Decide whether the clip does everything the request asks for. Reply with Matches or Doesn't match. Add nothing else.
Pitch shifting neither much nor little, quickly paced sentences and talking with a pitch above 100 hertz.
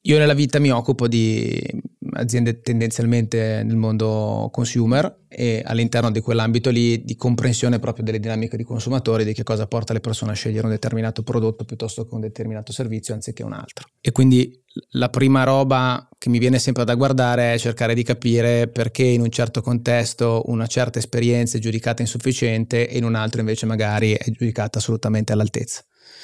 Doesn't match